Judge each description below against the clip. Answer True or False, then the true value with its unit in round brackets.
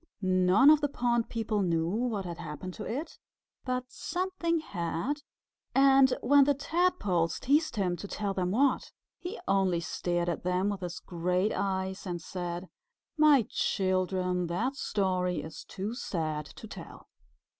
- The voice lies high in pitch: True (195 Hz)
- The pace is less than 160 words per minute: True (150 wpm)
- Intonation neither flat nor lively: False (6.5 semitones)